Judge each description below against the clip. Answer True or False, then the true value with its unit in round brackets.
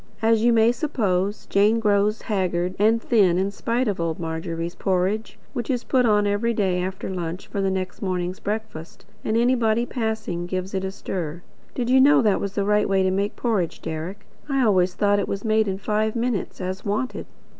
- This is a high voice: True (205 Hz)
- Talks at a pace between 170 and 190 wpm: False (200 wpm)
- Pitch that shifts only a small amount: False (3.2 semitones)